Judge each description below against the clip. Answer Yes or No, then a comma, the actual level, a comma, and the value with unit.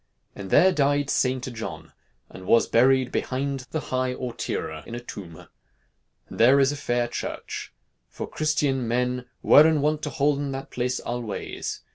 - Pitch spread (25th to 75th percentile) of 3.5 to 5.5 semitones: No, average, 2.8 semitones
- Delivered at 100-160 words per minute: Yes, average, 155 wpm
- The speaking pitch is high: No, low, 130 Hz